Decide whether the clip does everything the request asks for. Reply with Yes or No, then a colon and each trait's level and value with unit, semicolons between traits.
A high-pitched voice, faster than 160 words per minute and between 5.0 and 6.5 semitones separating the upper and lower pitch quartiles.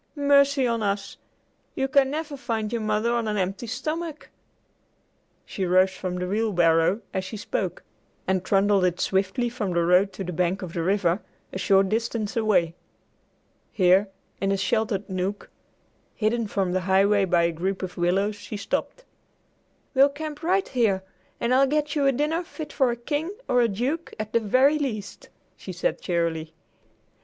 Yes: high, 210 Hz; average, 170 wpm; wide, 5.6 semitones